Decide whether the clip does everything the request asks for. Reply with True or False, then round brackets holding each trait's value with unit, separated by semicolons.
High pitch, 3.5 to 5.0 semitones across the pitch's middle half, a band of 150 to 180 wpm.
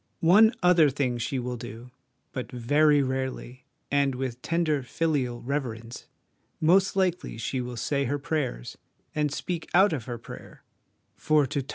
False (135 Hz; 3.9 semitones; 165 wpm)